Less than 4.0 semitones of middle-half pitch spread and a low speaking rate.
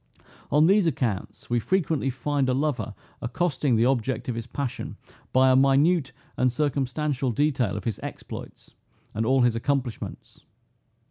No: average, 3.4 semitones; average, 145 wpm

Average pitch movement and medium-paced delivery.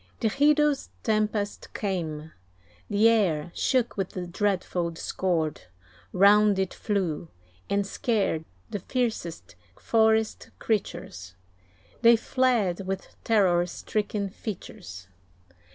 No: average, 4.1 semitones; slow, 100 wpm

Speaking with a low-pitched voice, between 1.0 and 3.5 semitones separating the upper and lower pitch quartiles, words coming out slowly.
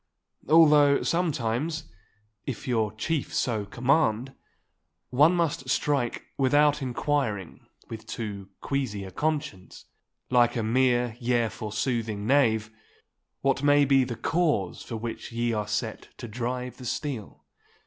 No: low, 125 Hz; average, 4.5 semitones; slow, 125 wpm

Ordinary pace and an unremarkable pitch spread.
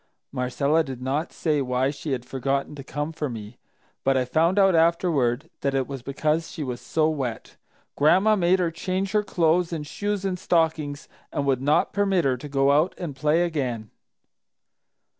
Yes: average, 180 wpm; average, 4.1 semitones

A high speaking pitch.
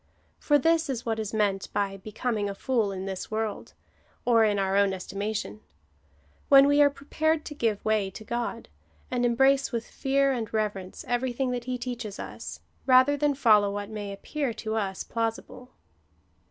Yes: high, 225 Hz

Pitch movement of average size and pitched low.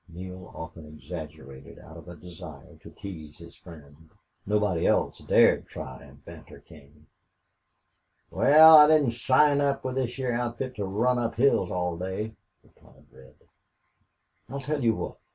No: wide, 8.2 semitones; very low, 95 Hz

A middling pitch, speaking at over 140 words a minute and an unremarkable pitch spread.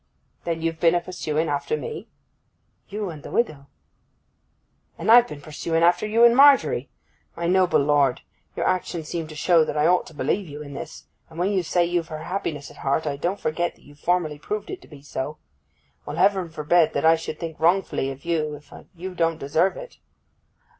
Yes: medium, 165 Hz; average, 200 wpm; average, 3.4 semitones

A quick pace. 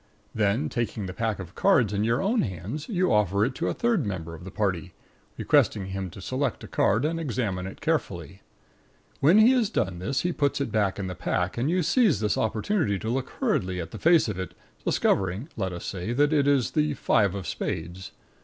Yes: fast, 215 wpm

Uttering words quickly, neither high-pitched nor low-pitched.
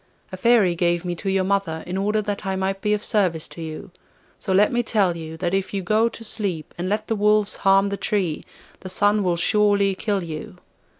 No: fast, 225 wpm; high, 195 Hz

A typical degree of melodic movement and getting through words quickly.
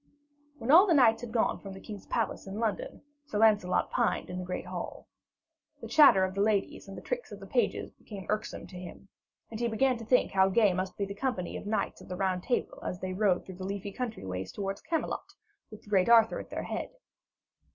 Yes: average, 3.3 semitones; fast, 235 wpm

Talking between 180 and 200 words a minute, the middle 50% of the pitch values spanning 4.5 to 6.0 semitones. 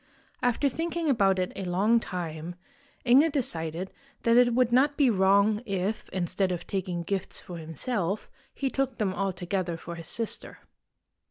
No: average, 155 wpm; wide, 5.4 semitones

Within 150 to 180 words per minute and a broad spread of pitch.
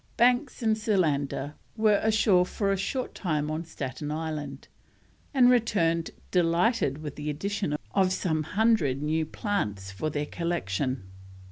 No: slow, 135 wpm; wide, 6.1 semitones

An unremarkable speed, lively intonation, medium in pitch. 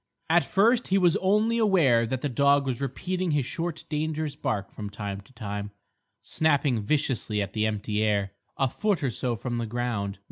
No: average, 185 wpm; wide, 6.8 semitones; low, 130 Hz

